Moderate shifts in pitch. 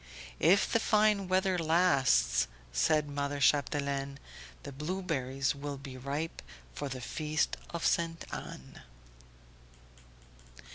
Yes: average, 3.7 semitones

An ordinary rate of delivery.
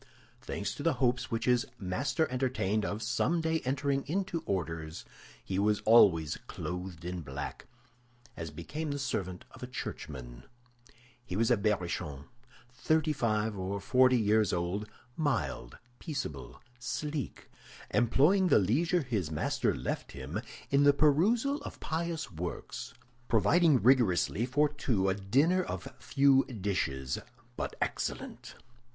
No: slow, 130 wpm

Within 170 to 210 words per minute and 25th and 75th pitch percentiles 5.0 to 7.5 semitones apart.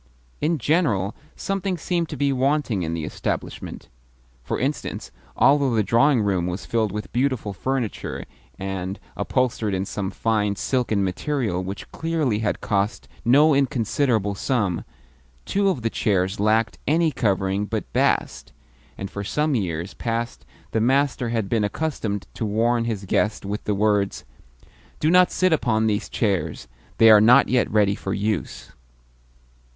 No: average, 150 wpm; average, 5.3 semitones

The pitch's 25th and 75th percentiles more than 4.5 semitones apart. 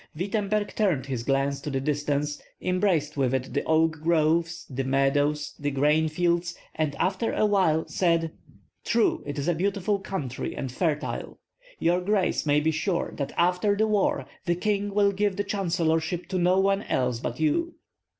Yes: average, 5.0 semitones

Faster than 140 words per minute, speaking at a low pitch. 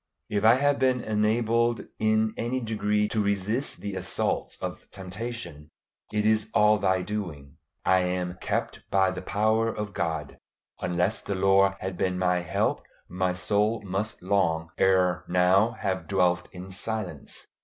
Yes: average, 150 wpm; low, 100 Hz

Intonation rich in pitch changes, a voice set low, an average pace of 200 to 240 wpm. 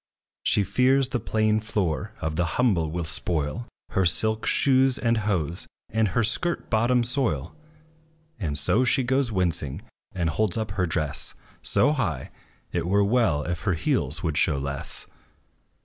No: wide, 6.3 semitones; low, 100 Hz; average, 155 wpm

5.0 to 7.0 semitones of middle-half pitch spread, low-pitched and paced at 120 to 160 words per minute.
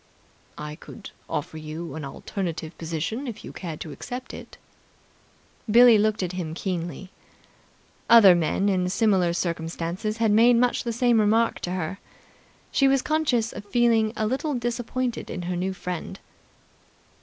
No: wide, 5.4 semitones; high, 200 Hz; average, 150 wpm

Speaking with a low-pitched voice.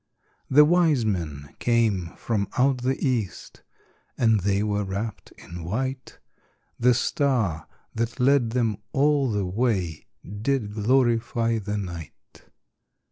Yes: low, 115 Hz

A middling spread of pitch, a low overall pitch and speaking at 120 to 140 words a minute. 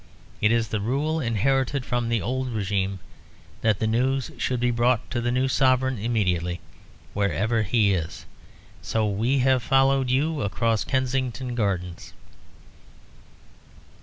Yes: average, 3.8 semitones; low, 120 Hz; slow, 135 wpm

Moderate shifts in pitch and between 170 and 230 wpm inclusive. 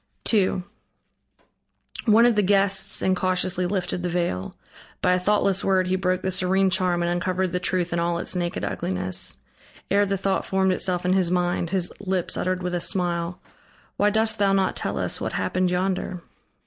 No: narrow, 1.5 semitones; average, 180 wpm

